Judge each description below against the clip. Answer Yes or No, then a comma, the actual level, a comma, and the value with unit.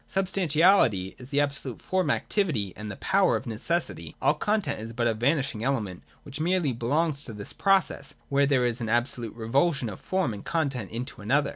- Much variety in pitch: Yes, wide, 6.5 semitones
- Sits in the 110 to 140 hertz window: Yes, low, 135 Hz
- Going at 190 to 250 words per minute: Yes, average, 195 wpm